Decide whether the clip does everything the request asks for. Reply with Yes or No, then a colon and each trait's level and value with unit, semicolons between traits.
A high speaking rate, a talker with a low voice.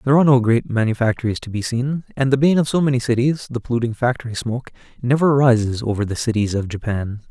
Yes: fast, 215 wpm; low, 120 Hz